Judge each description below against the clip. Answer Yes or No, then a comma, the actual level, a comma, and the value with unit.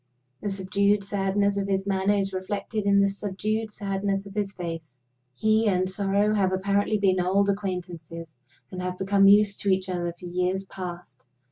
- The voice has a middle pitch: No, high, 195 Hz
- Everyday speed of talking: Yes, average, 170 wpm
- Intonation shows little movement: Yes, narrow, 1.6 semitones